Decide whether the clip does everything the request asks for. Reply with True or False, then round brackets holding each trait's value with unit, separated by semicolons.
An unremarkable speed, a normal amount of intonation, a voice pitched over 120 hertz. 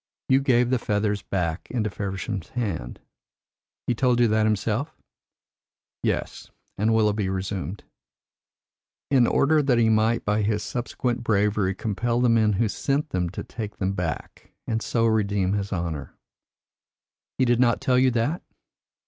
False (150 wpm; 3.3 semitones; 110 Hz)